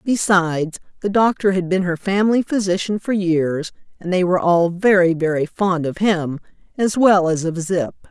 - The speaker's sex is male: No, female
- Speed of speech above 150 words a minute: Yes, average, 180 wpm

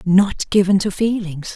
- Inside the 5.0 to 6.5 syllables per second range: No, 4.1 syllables/s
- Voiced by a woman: Yes, female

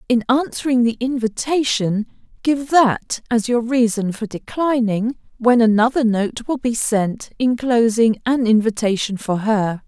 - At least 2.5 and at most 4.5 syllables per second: Yes, 4.1 syllables/s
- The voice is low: No, high, 235 Hz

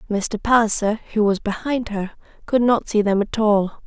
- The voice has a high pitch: Yes, high, 215 Hz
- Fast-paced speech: No, average, 185 wpm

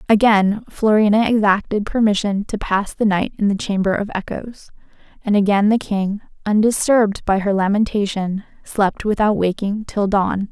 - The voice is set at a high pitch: Yes, high, 205 Hz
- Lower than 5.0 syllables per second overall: Yes, 4.8 syllables/s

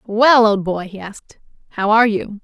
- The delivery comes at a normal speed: Yes, average, 195 wpm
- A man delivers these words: No, female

